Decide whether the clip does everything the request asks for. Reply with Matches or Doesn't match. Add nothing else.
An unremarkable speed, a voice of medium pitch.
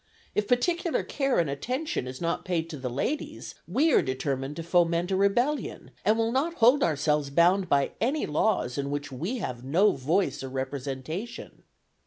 Matches